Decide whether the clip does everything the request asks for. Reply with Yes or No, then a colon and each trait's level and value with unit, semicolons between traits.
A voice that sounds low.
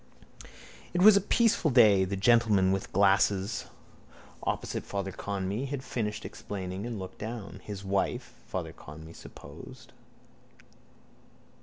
Yes: low, 100 Hz